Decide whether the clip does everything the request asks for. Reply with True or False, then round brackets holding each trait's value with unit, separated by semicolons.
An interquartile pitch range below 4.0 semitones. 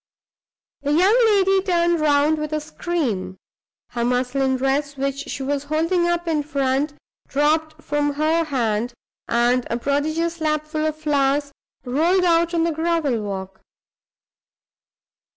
True (3.4 semitones)